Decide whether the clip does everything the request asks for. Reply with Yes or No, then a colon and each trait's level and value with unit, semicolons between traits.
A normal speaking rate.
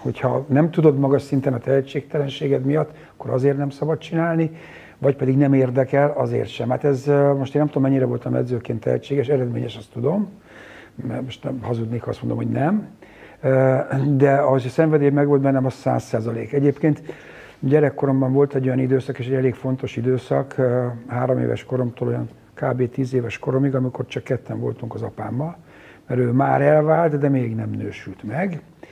No: fast, 175 wpm